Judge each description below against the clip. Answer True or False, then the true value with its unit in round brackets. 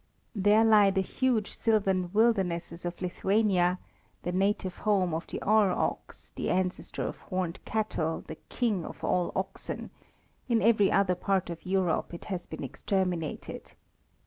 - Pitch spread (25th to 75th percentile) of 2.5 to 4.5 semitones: True (2.9 semitones)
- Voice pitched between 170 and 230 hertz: True (190 Hz)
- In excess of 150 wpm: False (145 wpm)